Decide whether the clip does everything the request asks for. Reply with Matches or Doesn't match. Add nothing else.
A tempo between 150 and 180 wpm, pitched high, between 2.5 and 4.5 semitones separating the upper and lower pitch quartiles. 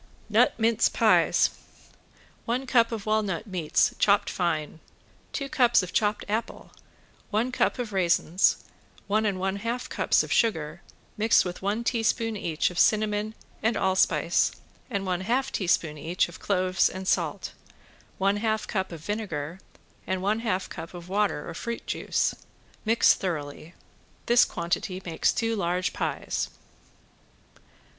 Doesn't match